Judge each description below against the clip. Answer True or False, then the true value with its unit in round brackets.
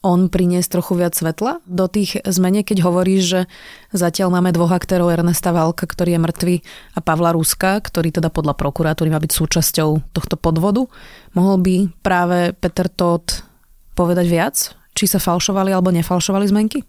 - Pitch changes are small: True (2.0 semitones)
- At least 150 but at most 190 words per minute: True (160 wpm)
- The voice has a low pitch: False (180 Hz)